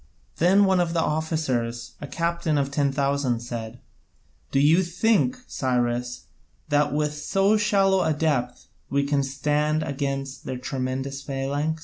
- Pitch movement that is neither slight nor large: Yes, average, 3.3 semitones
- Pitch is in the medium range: Yes, medium, 145 Hz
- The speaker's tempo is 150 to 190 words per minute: No, average, 140 wpm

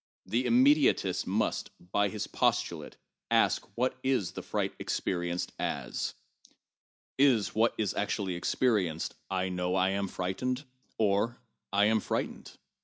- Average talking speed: No, slow, 130 wpm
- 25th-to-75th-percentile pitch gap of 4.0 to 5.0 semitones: Yes, average, 4.5 semitones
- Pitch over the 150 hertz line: No, low, 100 Hz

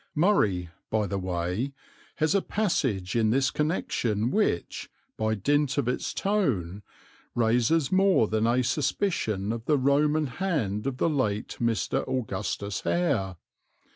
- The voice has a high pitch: No, low, 125 Hz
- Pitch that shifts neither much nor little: No, wide, 6.5 semitones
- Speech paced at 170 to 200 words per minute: No, slow, 135 wpm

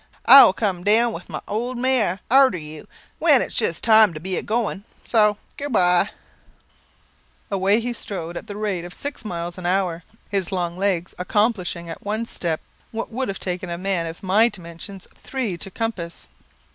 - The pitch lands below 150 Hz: No, high, 195 Hz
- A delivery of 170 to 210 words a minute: Yes, average, 185 wpm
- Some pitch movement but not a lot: Yes, average, 4.0 semitones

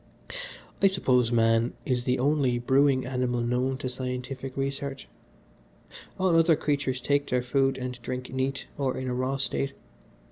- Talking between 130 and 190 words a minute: Yes, average, 150 wpm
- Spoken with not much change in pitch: Yes, narrow, 1.6 semitones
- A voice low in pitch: Yes, low, 130 Hz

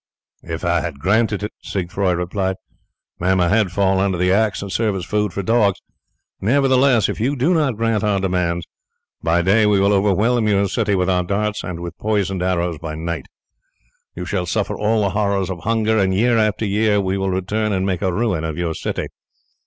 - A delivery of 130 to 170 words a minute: No, average, 200 wpm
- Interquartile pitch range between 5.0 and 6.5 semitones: No, average, 3.0 semitones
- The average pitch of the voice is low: Yes, low, 100 Hz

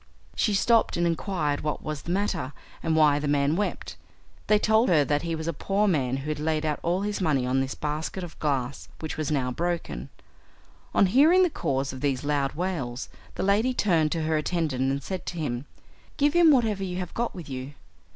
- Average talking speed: No, fast, 210 wpm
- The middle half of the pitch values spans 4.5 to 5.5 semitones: Yes, average, 5.2 semitones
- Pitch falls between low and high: Yes, medium, 160 Hz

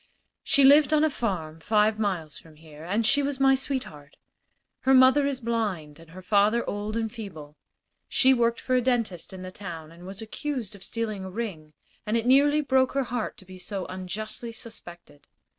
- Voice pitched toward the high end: Yes, high, 215 Hz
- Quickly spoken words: No, average, 195 wpm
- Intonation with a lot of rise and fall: Yes, wide, 5.8 semitones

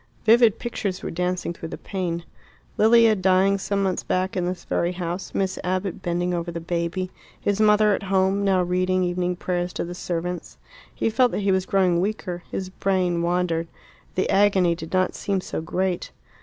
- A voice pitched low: No, medium, 185 Hz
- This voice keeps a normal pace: Yes, average, 185 wpm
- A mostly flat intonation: Yes, narrow, 1.8 semitones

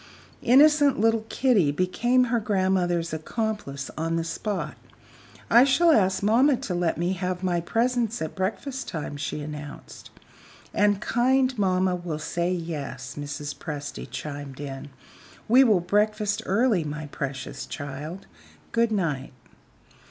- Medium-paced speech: No, slow, 130 wpm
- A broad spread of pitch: Yes, wide, 6.8 semitones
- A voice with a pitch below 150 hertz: No, medium, 185 Hz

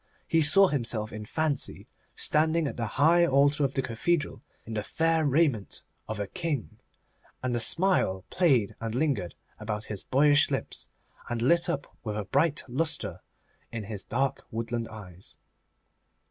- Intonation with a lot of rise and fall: Yes, wide, 6.2 semitones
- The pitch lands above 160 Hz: No, low, 135 Hz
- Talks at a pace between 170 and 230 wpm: No, average, 150 wpm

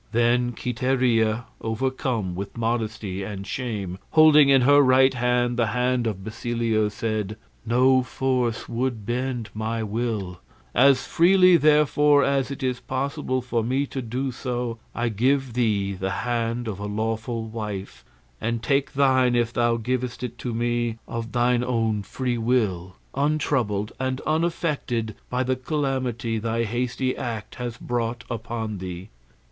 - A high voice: No, low, 120 Hz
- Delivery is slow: No, average, 145 wpm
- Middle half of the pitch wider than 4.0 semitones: No, narrow, 2.6 semitones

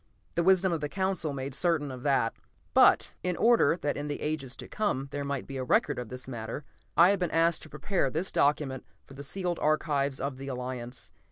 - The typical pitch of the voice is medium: Yes, medium, 145 Hz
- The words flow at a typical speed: No, fast, 215 wpm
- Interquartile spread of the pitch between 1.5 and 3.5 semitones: No, average, 4.2 semitones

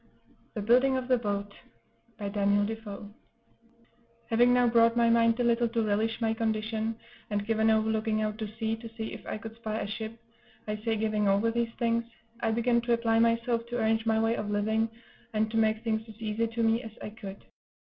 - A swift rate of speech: Yes, fast, 210 wpm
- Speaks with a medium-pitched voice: No, high, 225 Hz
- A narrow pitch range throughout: Yes, narrow, 1.3 semitones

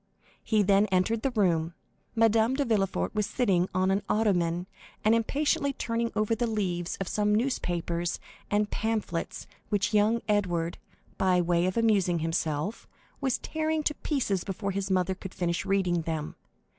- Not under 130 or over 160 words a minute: Yes, average, 155 wpm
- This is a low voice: No, high, 200 Hz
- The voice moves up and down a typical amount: Yes, average, 4.2 semitones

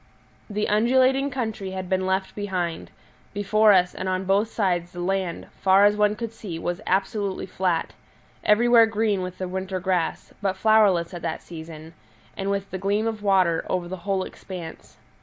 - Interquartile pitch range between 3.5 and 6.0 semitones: No, narrow, 2.6 semitones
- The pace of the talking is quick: No, average, 175 wpm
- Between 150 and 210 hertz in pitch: Yes, high, 190 Hz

